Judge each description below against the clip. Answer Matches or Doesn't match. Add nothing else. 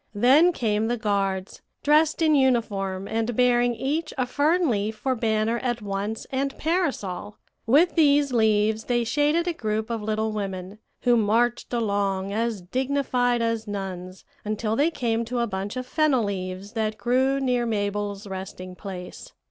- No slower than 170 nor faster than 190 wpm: Doesn't match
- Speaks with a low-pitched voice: Doesn't match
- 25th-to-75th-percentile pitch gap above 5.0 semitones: Doesn't match